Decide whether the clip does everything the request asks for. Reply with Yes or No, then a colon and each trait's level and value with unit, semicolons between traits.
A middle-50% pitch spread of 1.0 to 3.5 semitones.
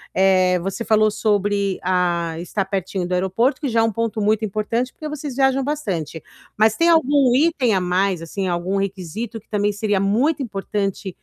No: average, 3.9 semitones